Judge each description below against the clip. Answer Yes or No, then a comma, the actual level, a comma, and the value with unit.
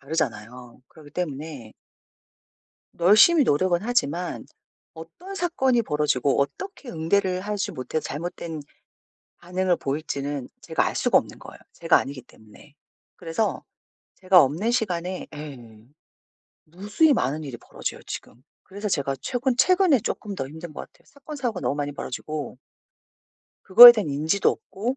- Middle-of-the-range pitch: Yes, medium, 170 Hz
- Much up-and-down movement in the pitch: Yes, wide, 6.8 semitones